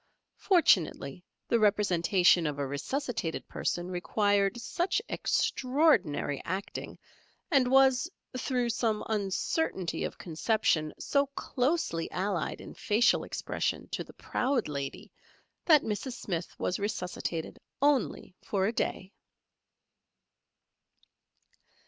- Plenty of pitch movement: Yes, wide, 6.5 semitones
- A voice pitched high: Yes, high, 205 Hz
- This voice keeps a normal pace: No, slow, 100 wpm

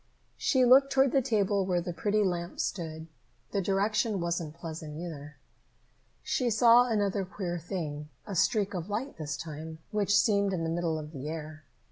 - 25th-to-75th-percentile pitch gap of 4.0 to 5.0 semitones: Yes, average, 4.5 semitones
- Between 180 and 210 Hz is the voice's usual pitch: Yes, medium, 185 Hz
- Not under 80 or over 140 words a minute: No, average, 170 wpm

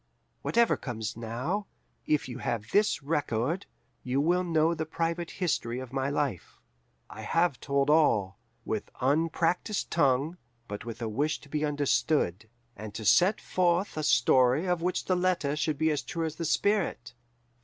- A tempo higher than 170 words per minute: No, average, 165 wpm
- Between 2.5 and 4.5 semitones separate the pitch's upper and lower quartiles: No, wide, 5.4 semitones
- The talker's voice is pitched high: No, medium, 150 Hz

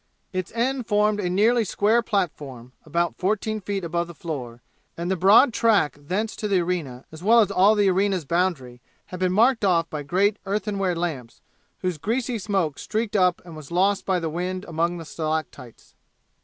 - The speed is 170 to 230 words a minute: Yes, average, 185 wpm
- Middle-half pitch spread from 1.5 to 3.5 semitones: No, average, 4.0 semitones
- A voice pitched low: No, medium, 185 Hz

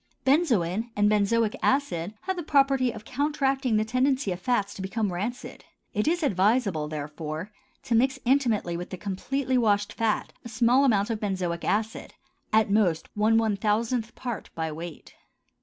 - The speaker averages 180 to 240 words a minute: No, average, 160 wpm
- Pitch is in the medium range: No, high, 220 Hz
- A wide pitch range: No, average, 4.8 semitones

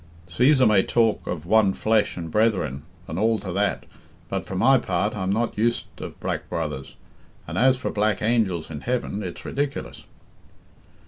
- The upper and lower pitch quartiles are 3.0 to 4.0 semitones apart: No, average, 4.5 semitones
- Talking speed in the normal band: Yes, average, 170 wpm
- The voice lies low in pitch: Yes, low, 105 Hz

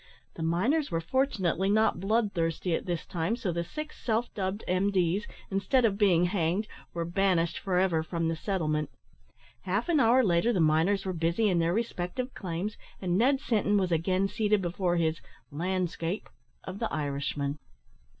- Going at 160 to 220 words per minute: Yes, average, 165 wpm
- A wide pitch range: No, average, 4.0 semitones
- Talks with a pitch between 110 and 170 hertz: No, medium, 185 Hz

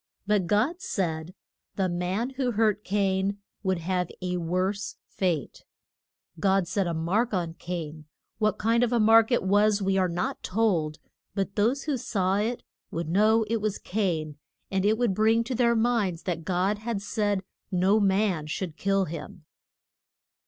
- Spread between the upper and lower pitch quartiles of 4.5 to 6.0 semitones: No, average, 3.4 semitones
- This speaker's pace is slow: No, average, 165 wpm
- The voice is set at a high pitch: Yes, high, 195 Hz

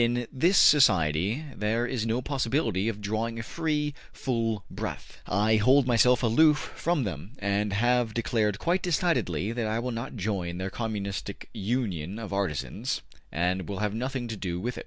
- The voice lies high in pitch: No, low, 110 Hz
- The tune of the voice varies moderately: Yes, average, 4.0 semitones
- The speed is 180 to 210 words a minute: No, average, 170 wpm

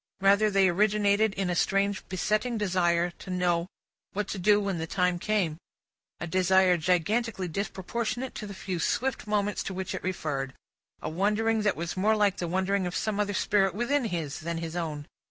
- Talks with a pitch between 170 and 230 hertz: Yes, high, 190 Hz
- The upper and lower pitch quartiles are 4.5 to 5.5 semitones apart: No, average, 3.1 semitones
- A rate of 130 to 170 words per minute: No, average, 185 wpm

